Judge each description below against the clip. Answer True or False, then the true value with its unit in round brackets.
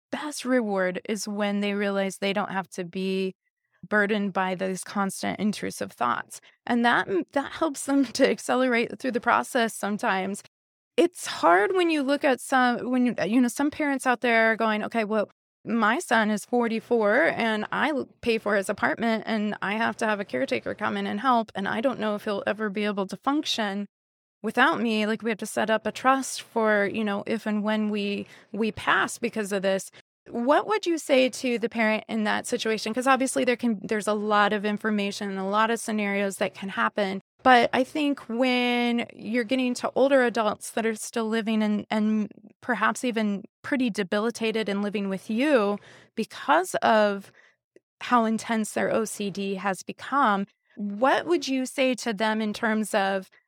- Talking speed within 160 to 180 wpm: False (190 wpm)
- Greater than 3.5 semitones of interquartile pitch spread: False (3.1 semitones)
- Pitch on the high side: True (220 Hz)